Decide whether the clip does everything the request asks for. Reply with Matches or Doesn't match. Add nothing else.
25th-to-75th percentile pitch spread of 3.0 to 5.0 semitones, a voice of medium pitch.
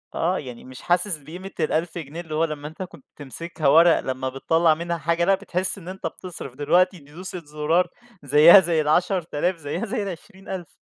Matches